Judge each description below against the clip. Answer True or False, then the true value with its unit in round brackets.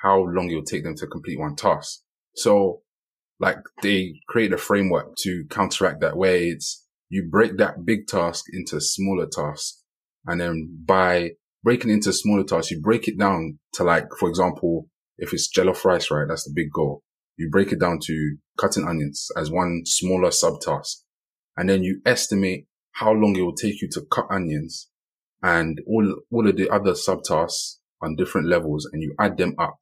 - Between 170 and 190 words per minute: True (185 wpm)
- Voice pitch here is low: True (90 Hz)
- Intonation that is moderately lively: True (3.1 semitones)